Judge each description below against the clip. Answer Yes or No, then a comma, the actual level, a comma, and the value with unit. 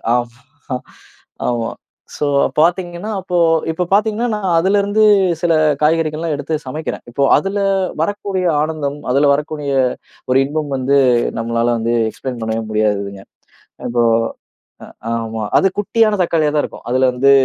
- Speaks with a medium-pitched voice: Yes, medium, 150 Hz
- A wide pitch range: Yes, wide, 6.2 semitones